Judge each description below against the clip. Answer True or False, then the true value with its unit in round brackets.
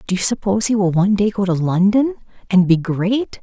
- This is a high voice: True (200 Hz)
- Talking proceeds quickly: True (225 wpm)